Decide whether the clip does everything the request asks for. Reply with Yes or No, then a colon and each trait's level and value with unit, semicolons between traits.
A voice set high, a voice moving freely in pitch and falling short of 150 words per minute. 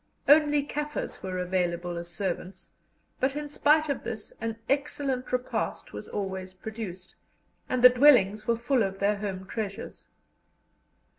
Yes: high, 220 Hz; wide, 6.5 semitones; average, 140 wpm